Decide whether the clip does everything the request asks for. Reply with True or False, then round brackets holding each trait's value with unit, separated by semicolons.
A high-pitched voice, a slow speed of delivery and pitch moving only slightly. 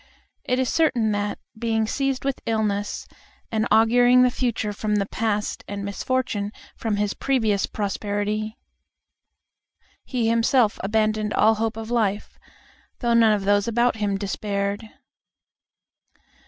True (220 Hz; 125 wpm; 2.3 semitones)